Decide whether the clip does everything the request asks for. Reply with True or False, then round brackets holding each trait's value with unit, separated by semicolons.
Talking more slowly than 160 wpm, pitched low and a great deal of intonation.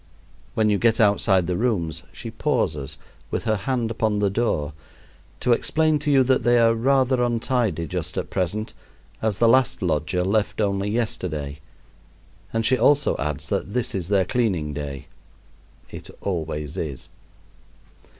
True (150 wpm; 105 Hz; 6.1 semitones)